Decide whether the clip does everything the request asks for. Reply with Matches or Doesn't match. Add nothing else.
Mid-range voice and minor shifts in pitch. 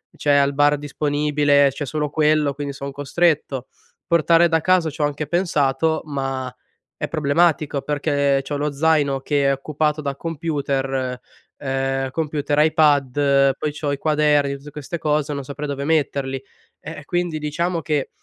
Matches